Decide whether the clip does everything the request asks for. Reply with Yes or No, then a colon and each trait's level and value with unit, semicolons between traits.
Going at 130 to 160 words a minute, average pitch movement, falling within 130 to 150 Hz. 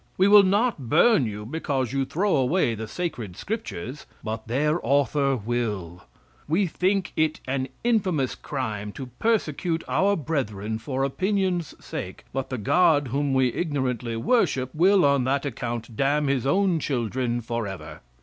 No: average, 150 wpm; wide, 6.4 semitones; medium, 140 Hz